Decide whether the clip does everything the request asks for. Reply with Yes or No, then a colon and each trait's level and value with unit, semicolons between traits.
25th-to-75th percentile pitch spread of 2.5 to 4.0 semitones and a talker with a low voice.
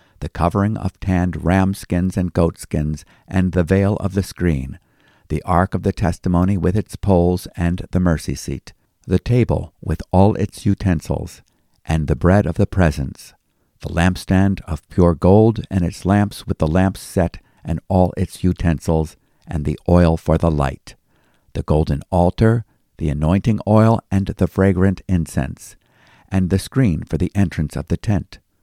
Yes: average, 3.0 semitones; very low, 90 Hz